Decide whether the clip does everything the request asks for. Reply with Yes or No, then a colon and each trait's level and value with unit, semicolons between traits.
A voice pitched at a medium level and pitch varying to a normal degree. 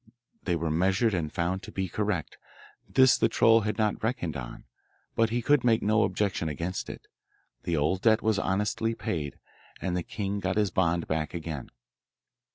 No: very low, 95 Hz; average, 4.5 semitones